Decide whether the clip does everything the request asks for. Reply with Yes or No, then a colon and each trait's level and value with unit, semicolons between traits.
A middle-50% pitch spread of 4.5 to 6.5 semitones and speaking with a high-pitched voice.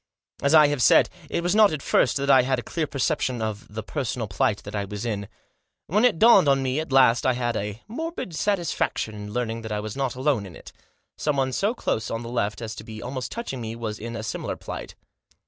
No: average, 5.2 semitones; low, 125 Hz